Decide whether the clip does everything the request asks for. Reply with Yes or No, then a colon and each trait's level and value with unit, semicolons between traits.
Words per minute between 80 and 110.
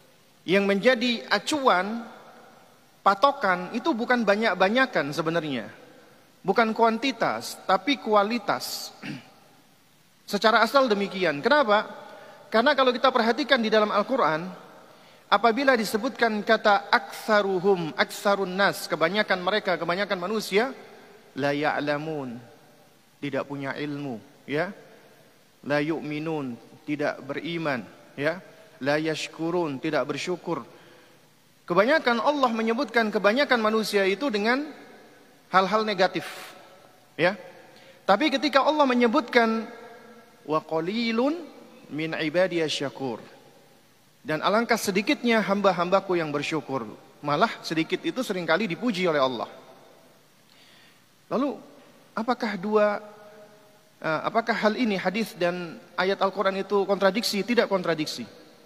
Yes: average, 95 wpm